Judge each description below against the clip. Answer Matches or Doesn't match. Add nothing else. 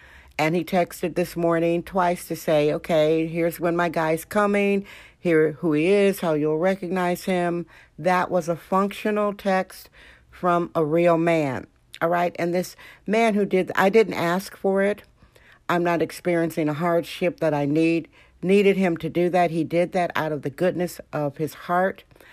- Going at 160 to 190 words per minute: Matches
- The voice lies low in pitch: Doesn't match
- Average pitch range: Doesn't match